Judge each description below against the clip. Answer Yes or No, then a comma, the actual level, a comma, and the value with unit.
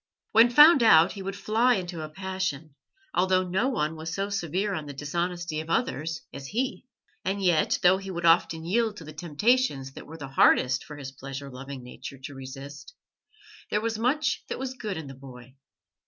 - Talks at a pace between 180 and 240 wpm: Yes, average, 195 wpm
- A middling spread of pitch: No, wide, 6.1 semitones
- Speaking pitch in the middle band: Yes, medium, 170 Hz